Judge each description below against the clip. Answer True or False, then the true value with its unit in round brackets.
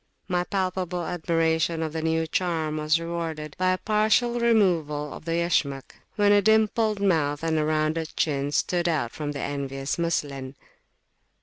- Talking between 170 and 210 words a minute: False (160 wpm)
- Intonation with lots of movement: False (3.3 semitones)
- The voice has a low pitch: False (165 Hz)